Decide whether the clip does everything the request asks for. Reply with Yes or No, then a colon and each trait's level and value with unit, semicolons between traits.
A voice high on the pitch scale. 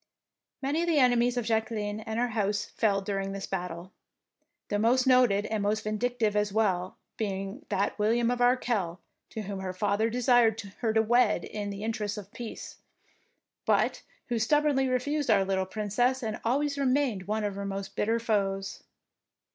Yes: high, 220 Hz